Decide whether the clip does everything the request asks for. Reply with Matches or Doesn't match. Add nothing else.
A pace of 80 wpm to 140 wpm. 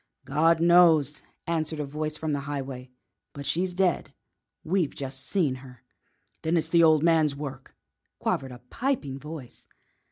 Doesn't match